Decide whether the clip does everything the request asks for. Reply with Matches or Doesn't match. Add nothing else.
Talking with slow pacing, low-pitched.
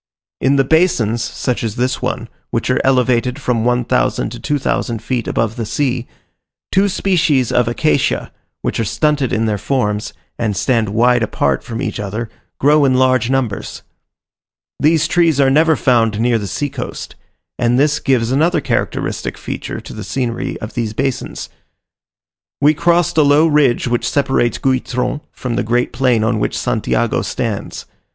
Doesn't match